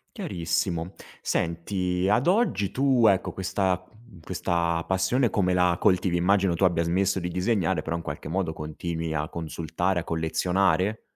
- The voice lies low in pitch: Yes, very low, 90 Hz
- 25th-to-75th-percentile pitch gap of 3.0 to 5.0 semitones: No, narrow, 2.5 semitones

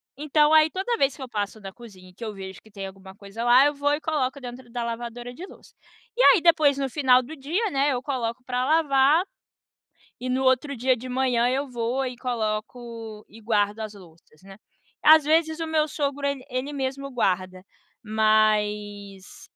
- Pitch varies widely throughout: No, average, 4.7 semitones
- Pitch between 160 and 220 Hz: No, very high, 250 Hz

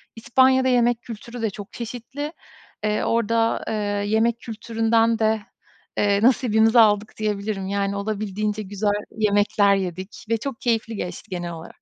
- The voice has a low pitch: No, high, 220 Hz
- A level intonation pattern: Yes, narrow, 2.3 semitones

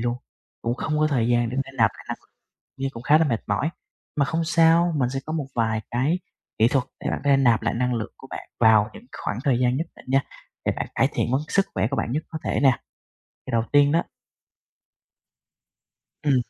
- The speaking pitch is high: No, low, 135 Hz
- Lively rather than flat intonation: No, average, 4.4 semitones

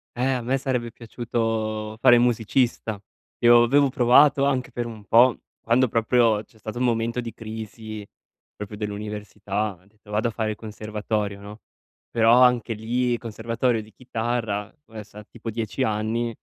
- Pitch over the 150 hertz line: No, low, 115 Hz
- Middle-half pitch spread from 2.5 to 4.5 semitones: No, narrow, 2.1 semitones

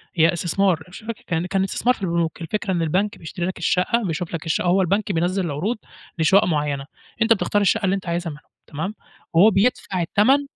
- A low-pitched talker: No, medium, 185 Hz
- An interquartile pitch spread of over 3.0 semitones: Yes, average, 3.6 semitones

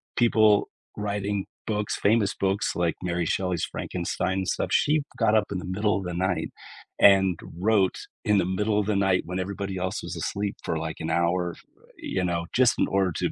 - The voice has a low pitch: Yes, very low, 95 Hz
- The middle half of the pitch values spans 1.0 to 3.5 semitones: Yes, narrow, 2.4 semitones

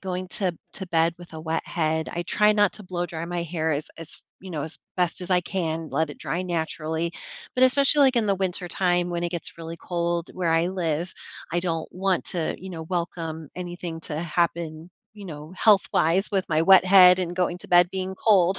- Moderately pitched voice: Yes, medium, 175 Hz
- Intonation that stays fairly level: Yes, narrow, 2.3 semitones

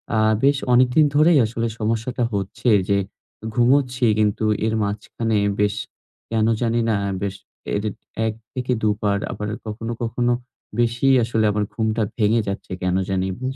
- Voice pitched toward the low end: Yes, low, 115 Hz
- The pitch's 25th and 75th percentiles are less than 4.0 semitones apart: Yes, average, 2.9 semitones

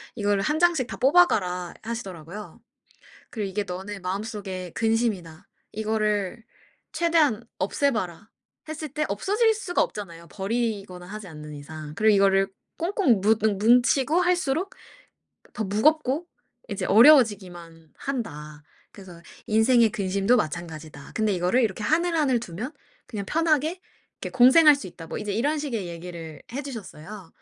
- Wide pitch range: Yes, wide, 6.6 semitones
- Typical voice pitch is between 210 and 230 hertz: Yes, high, 215 Hz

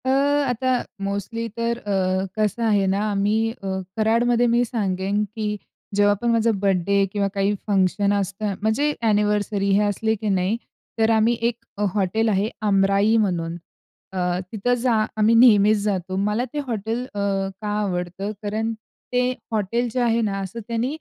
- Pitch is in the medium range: No, high, 210 Hz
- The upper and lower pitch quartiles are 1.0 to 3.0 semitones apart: Yes, narrow, 2.6 semitones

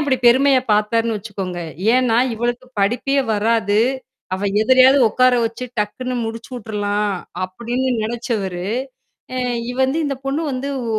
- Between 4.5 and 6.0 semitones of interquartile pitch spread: No, average, 3.6 semitones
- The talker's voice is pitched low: No, high, 235 Hz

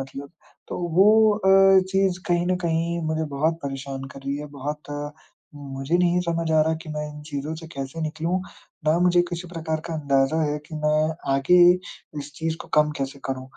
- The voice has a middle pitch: Yes, medium, 155 Hz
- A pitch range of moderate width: Yes, average, 3.5 semitones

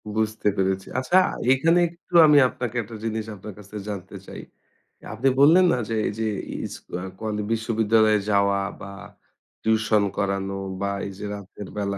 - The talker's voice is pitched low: Yes, low, 110 Hz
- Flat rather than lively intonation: Yes, narrow, 2.3 semitones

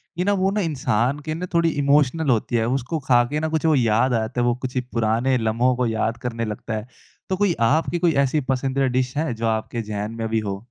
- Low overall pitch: Yes, low, 125 Hz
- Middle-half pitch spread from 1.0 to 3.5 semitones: No, average, 4.8 semitones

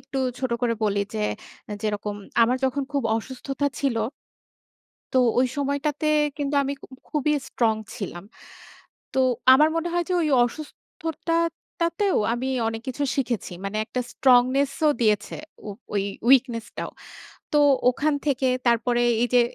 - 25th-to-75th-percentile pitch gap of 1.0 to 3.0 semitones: No, average, 3.8 semitones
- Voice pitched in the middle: No, very high, 260 Hz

